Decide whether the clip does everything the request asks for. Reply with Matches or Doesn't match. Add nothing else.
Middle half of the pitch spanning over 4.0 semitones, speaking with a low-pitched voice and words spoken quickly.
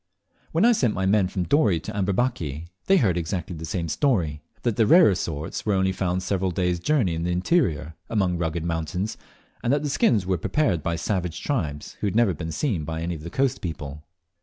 Matches